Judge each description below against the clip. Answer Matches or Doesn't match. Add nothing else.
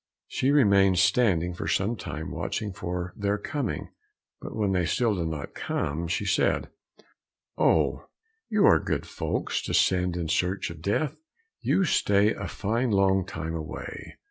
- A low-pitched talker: Matches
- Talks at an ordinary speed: Matches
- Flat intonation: Doesn't match